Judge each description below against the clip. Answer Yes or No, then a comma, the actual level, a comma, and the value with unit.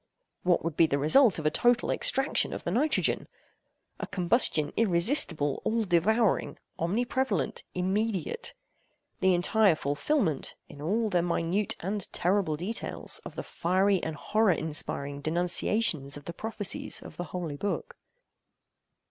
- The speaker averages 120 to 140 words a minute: Yes, slow, 135 wpm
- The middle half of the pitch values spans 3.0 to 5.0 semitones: No, wide, 5.4 semitones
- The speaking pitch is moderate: Yes, medium, 180 Hz